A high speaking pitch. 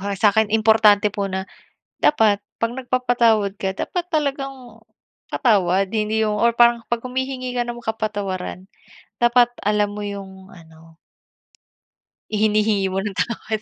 Yes: high, 215 Hz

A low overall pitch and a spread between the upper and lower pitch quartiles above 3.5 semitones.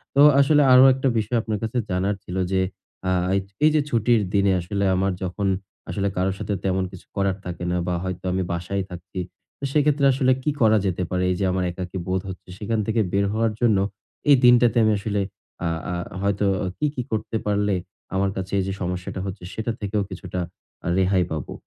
No: low, 100 Hz; average, 3.2 semitones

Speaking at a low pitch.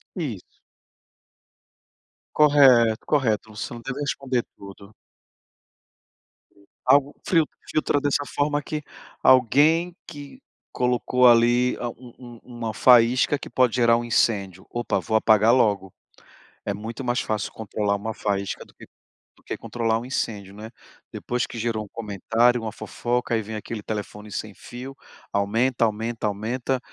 Yes: low, 120 Hz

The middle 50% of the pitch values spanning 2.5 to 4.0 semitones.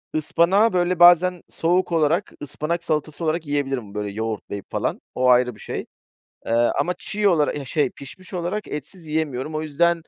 No: average, 4.5 semitones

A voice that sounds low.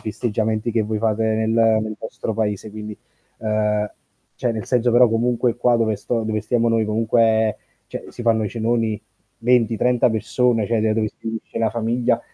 Yes: low, 110 Hz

